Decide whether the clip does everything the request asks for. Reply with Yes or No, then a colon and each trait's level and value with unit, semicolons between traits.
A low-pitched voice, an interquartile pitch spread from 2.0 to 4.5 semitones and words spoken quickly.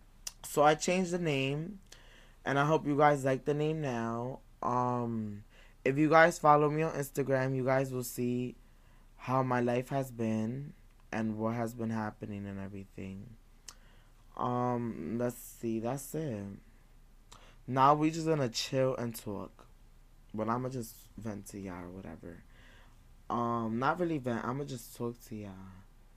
No: low, 120 Hz; average, 3.5 semitones; average, 155 wpm